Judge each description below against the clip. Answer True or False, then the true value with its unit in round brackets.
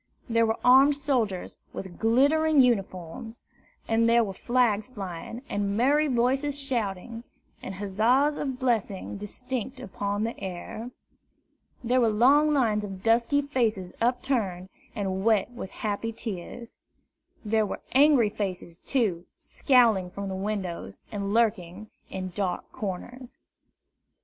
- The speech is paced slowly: True (125 wpm)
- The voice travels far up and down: False (4.3 semitones)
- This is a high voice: True (225 Hz)